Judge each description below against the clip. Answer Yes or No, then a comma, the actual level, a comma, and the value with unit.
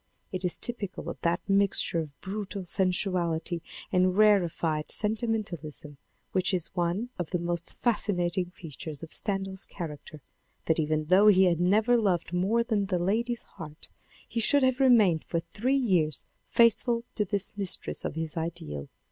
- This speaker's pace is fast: No, average, 155 wpm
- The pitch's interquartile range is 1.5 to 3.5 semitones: No, average, 4.0 semitones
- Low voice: No, medium, 185 Hz